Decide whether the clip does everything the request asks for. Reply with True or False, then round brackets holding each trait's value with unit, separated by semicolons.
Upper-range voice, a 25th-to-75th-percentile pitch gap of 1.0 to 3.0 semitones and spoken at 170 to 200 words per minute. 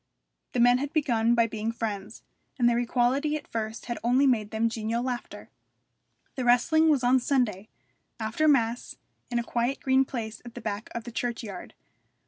True (240 Hz; 2.4 semitones; 175 wpm)